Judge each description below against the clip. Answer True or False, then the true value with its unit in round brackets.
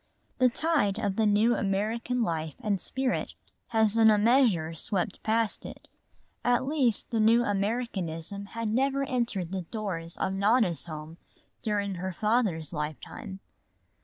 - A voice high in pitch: True (210 Hz)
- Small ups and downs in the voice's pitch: False (3.9 semitones)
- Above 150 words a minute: False (140 wpm)